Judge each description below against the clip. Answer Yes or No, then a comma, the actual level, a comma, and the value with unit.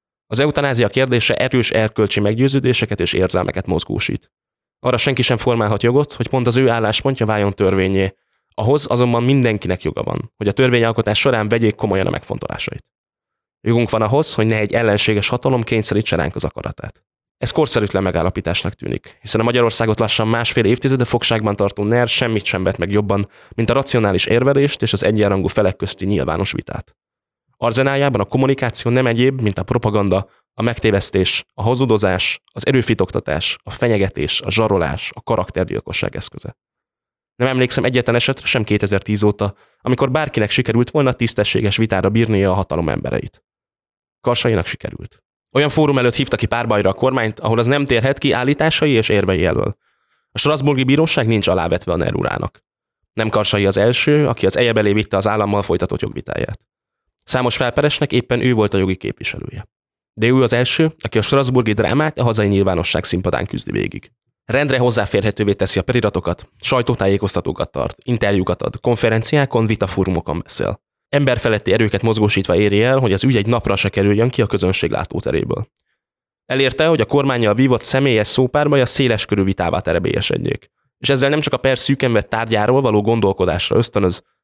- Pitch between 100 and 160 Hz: Yes, low, 115 Hz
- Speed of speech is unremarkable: No, fast, 160 wpm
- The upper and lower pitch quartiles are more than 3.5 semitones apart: Yes, average, 4.0 semitones